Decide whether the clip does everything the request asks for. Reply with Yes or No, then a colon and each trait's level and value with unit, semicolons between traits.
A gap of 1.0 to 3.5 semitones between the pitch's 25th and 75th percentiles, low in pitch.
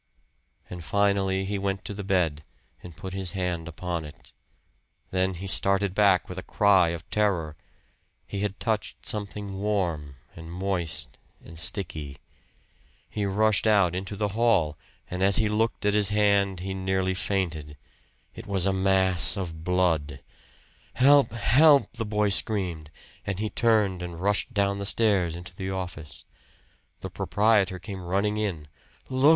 Yes: average, 2.9 semitones; very low, 95 Hz